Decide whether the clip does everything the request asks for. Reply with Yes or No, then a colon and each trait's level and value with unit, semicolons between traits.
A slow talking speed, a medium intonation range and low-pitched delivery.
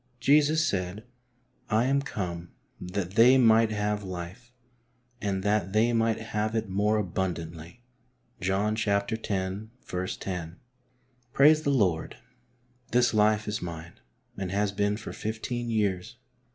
Yes: slow, 125 wpm; average, 3.4 semitones; low, 105 Hz